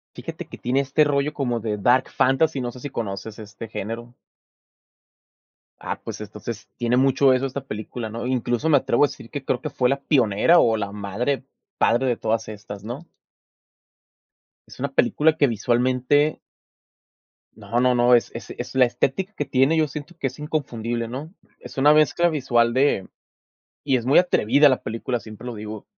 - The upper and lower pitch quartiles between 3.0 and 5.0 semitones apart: Yes, average, 3.7 semitones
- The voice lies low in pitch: Yes, low, 125 Hz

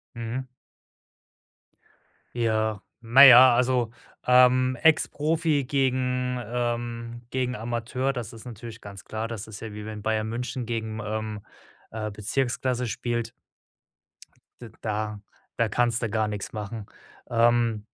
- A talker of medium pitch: No, low, 115 Hz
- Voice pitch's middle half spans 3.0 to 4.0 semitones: No, narrow, 2.4 semitones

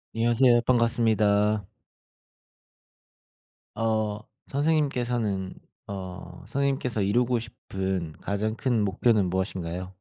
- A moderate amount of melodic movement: Yes, average, 4.0 semitones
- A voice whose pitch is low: Yes, low, 110 Hz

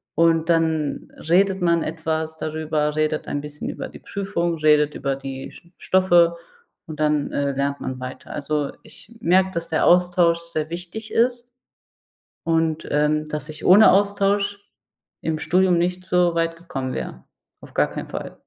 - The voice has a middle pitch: Yes, medium, 165 Hz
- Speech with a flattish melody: No, average, 3.0 semitones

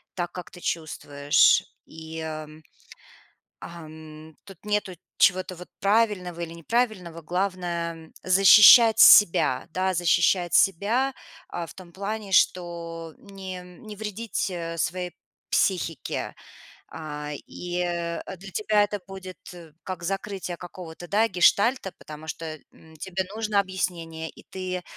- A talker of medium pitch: Yes, medium, 180 Hz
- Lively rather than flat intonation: No, average, 2.9 semitones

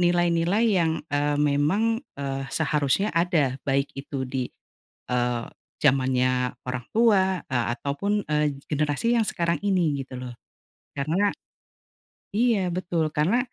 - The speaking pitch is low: No, medium, 150 Hz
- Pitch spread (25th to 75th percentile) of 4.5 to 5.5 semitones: Yes, average, 5.2 semitones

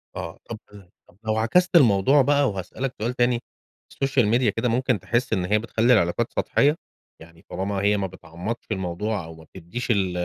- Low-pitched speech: Yes, low, 110 Hz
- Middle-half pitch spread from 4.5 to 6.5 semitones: Yes, average, 4.8 semitones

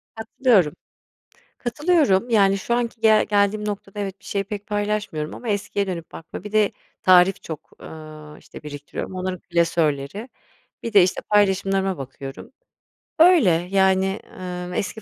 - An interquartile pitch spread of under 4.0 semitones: Yes, average, 3.0 semitones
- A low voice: No, high, 195 Hz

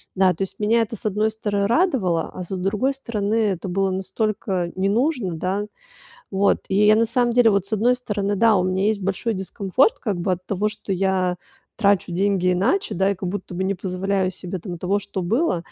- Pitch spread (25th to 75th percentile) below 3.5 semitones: Yes, average, 2.7 semitones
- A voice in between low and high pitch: No, high, 200 Hz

